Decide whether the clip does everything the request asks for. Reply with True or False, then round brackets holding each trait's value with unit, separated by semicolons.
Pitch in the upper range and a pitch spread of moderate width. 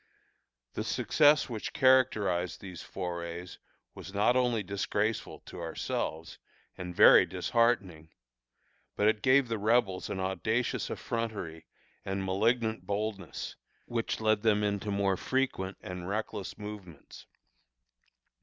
False (105 Hz; 3.6 semitones)